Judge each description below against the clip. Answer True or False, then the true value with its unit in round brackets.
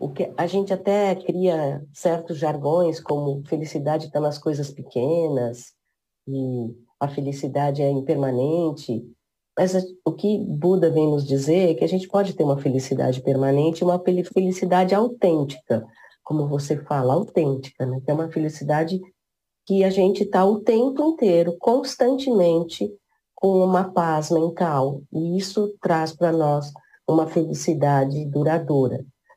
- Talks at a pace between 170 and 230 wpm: False (140 wpm)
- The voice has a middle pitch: True (160 Hz)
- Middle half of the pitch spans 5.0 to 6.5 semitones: False (4.5 semitones)